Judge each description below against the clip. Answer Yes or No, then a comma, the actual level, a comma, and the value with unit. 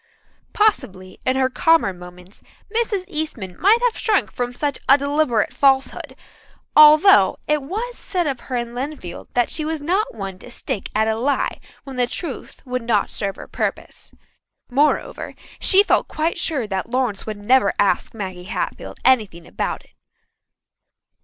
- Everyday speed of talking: Yes, average, 160 wpm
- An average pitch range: No, wide, 6.7 semitones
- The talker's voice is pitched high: Yes, very high, 260 Hz